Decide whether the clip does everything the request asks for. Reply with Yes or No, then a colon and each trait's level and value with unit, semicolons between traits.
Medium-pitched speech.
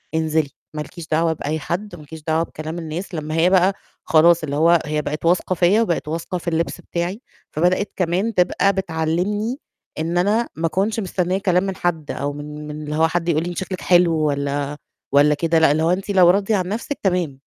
Yes: medium, 170 Hz